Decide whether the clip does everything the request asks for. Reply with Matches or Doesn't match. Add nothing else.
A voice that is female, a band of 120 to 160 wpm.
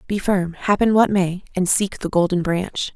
Doesn't match